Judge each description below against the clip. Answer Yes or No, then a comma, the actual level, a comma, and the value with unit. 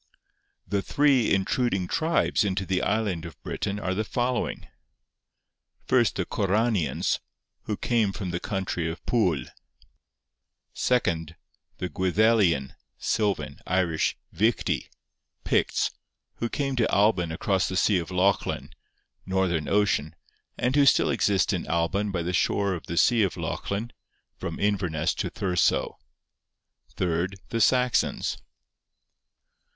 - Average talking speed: No, slow, 125 wpm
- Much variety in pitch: No, average, 4.0 semitones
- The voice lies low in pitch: Yes, very low, 95 Hz